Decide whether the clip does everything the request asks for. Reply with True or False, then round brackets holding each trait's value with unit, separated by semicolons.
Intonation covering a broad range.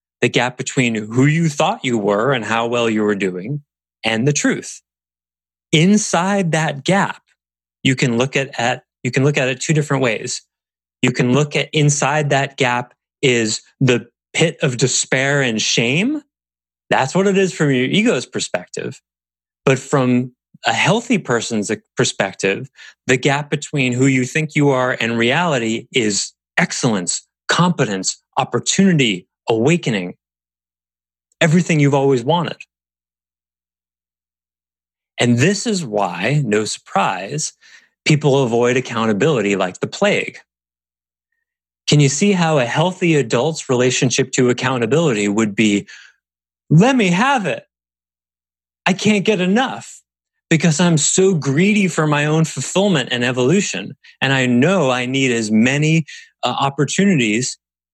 True (7.0 semitones)